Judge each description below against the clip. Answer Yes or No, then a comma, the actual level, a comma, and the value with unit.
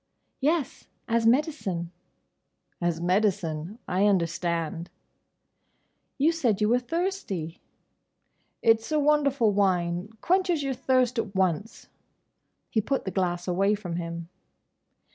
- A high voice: Yes, high, 205 Hz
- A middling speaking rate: No, slow, 105 wpm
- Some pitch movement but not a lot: No, wide, 7.0 semitones